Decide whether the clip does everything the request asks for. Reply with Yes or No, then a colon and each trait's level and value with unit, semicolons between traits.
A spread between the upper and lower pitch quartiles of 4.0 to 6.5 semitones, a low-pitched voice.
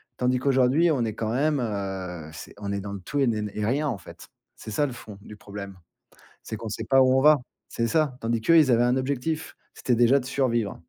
Yes: average, 4.4 semitones; low, 120 Hz